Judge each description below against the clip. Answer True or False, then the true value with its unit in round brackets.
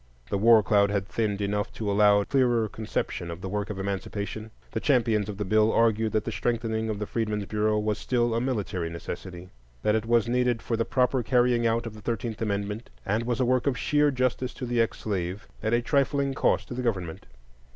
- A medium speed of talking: False (220 wpm)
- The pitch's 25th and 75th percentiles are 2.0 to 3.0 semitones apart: True (2.7 semitones)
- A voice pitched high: False (110 Hz)